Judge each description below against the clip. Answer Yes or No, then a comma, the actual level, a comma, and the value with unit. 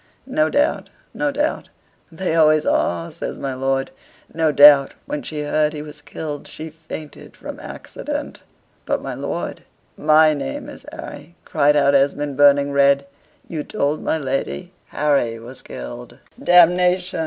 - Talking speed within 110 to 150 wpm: Yes, average, 145 wpm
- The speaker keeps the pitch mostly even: Yes, narrow, 2.3 semitones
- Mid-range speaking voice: Yes, medium, 150 Hz